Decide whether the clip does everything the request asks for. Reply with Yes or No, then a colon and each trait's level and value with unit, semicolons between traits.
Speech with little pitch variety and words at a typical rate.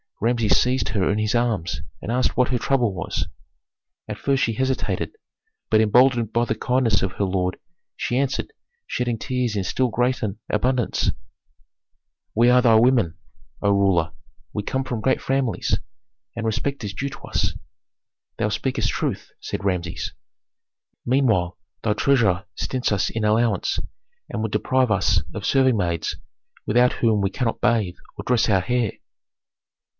No: average, 3.7 semitones; average, 155 wpm